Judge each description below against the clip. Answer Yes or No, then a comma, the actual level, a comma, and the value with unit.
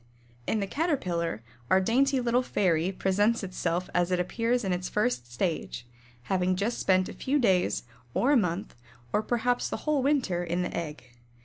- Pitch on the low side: No, high, 190 Hz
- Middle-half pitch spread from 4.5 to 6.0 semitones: Yes, wide, 5.4 semitones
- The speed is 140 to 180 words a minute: Yes, average, 175 wpm